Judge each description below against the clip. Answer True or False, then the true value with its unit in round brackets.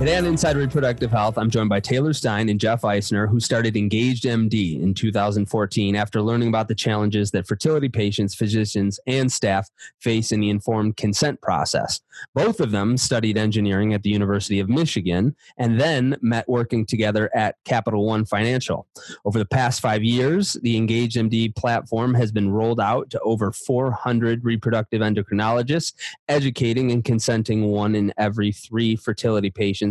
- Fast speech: False (165 wpm)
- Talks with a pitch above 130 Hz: False (110 Hz)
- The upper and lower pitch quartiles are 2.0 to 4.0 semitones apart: True (2.5 semitones)